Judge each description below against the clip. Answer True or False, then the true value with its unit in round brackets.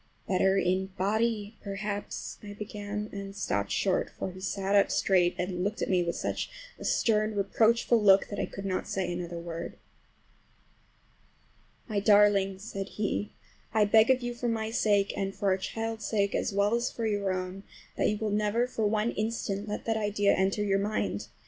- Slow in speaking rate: False (180 wpm)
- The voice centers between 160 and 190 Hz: False (205 Hz)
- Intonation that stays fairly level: True (1.9 semitones)